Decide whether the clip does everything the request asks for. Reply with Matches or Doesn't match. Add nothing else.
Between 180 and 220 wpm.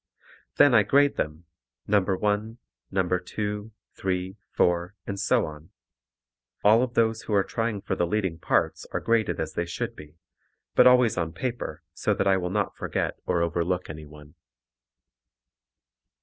Doesn't match